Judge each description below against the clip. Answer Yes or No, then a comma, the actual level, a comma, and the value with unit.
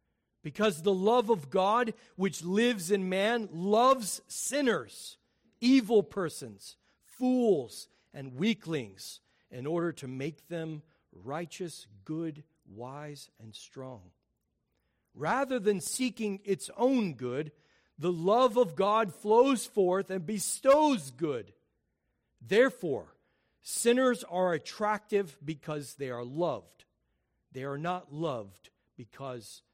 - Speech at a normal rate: No, slow, 110 wpm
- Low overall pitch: No, medium, 180 Hz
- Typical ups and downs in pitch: No, wide, 6.9 semitones